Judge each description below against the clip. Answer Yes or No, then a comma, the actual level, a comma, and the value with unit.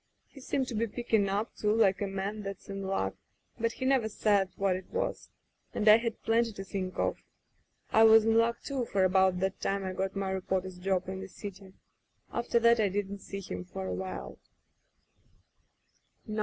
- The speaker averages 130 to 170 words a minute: No, average, 190 wpm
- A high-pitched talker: Yes, high, 195 Hz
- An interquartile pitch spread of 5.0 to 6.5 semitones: No, average, 2.8 semitones